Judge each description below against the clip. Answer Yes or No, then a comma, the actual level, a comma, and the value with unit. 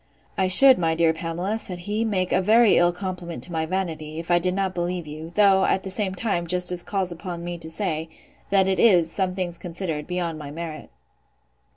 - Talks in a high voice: No, medium, 180 Hz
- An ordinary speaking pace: No, fast, 210 wpm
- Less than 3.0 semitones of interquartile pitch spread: Yes, narrow, 2.5 semitones